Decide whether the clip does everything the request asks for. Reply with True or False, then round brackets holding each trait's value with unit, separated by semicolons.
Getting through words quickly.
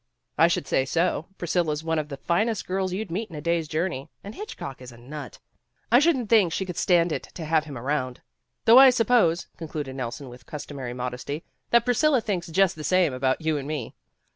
True (220 wpm)